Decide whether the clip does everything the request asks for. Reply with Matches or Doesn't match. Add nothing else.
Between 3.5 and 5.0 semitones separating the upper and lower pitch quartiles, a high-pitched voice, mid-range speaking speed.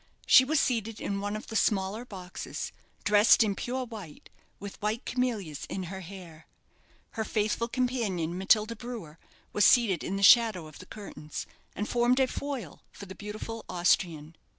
Matches